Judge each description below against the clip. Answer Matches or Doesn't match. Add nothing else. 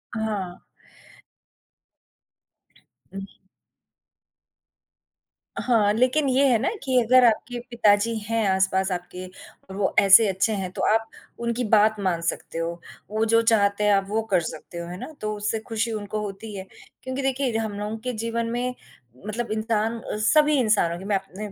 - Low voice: Doesn't match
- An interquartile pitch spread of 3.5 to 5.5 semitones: Doesn't match